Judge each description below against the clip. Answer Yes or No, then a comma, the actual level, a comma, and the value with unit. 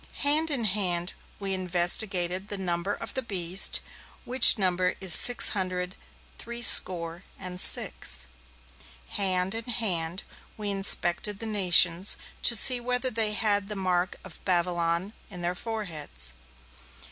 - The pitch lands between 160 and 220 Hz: Yes, high, 190 Hz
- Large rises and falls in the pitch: No, average, 3.4 semitones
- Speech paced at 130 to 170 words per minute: Yes, slow, 135 wpm